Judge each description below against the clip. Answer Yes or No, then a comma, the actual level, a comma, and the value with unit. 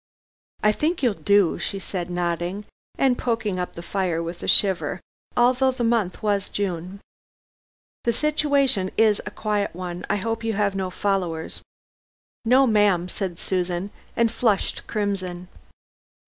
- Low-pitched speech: No, high, 200 Hz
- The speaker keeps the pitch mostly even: No, average, 3.9 semitones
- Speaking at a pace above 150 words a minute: No, average, 145 wpm